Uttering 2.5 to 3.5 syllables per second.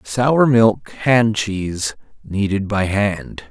Yes: 2.9 syllables/s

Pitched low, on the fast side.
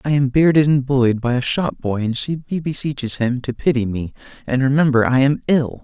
Yes: low, 130 Hz; fast, 215 wpm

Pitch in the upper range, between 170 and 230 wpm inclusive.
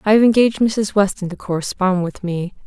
Yes: high, 195 Hz; average, 200 wpm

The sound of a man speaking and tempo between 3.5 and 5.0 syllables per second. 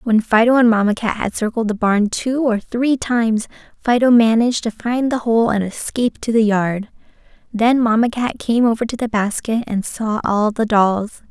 No: female; 4.8 syllables/s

